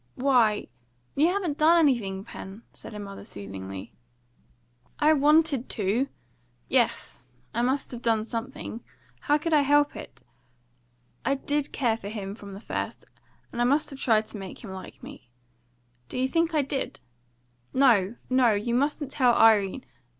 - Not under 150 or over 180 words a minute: Yes, average, 160 wpm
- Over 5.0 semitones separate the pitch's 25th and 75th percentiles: Yes, wide, 5.4 semitones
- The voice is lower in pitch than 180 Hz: No, high, 245 Hz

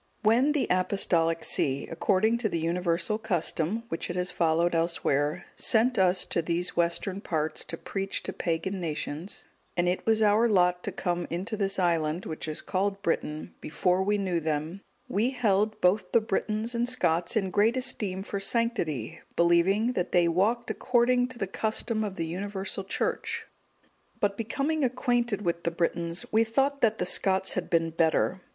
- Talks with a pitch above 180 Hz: Yes, high, 190 Hz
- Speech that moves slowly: No, average, 170 wpm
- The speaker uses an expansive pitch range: No, average, 4.4 semitones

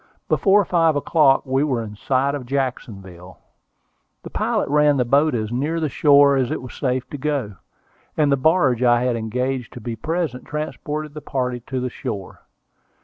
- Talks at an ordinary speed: Yes, average, 180 wpm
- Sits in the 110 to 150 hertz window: Yes, low, 135 Hz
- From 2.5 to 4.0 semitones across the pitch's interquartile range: Yes, average, 3.3 semitones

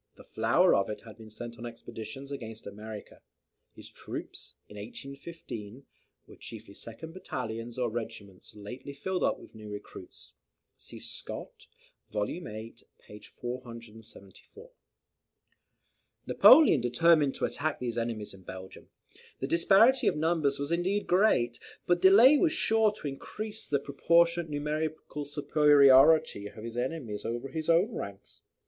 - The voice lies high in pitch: No, low, 135 Hz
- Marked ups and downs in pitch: Yes, wide, 6.9 semitones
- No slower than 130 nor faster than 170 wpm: Yes, average, 140 wpm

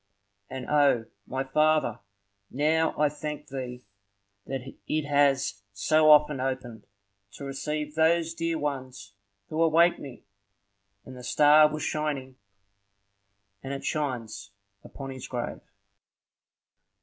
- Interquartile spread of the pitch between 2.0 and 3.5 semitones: Yes, average, 2.8 semitones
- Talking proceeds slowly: Yes, slow, 115 wpm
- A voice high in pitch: No, medium, 145 Hz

